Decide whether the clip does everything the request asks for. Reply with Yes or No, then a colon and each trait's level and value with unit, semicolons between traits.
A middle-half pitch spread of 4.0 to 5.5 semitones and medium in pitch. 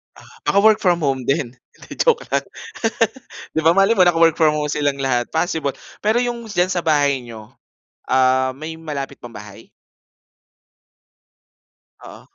Yes: average, 5.1 semitones; medium, 150 Hz